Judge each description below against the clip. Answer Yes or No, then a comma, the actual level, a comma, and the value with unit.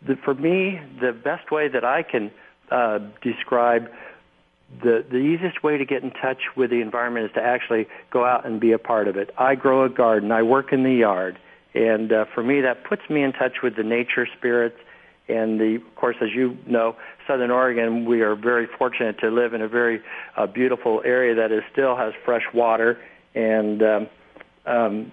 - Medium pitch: No, low, 120 Hz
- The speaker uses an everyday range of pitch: No, narrow, 2.3 semitones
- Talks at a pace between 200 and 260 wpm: Yes, fast, 205 wpm